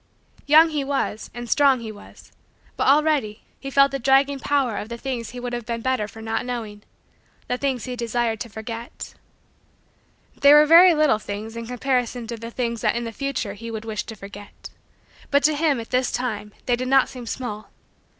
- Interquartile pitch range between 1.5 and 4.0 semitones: Yes, average, 3.5 semitones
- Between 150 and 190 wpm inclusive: No, average, 200 wpm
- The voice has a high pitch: Yes, high, 245 Hz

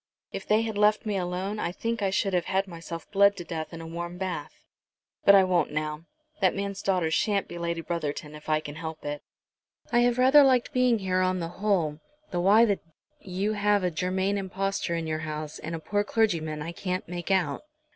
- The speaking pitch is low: No, medium, 185 Hz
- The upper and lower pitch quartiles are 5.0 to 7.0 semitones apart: No, average, 3.4 semitones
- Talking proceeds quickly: Yes, fast, 220 wpm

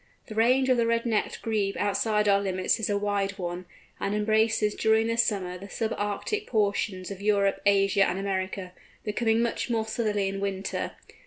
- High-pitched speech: Yes, high, 205 Hz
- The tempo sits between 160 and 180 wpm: Yes, average, 175 wpm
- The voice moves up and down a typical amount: No, narrow, 2.2 semitones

